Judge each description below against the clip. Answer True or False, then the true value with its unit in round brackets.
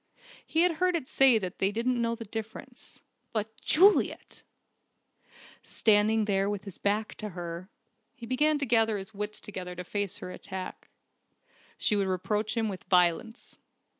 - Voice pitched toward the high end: True (215 Hz)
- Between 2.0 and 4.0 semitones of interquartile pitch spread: True (3.3 semitones)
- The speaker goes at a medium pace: True (160 wpm)